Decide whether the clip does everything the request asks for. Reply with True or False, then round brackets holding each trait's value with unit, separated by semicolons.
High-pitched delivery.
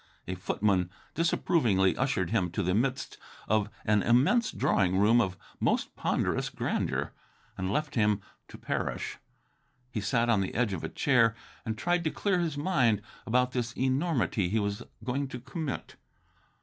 False (115 Hz)